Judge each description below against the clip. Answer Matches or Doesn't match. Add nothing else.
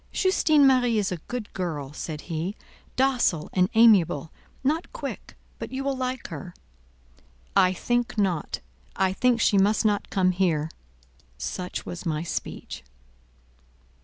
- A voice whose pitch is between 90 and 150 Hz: Doesn't match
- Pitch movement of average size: Doesn't match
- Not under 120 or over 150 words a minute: Matches